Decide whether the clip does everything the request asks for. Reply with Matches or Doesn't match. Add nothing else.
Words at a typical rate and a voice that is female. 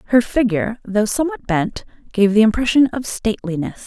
Matches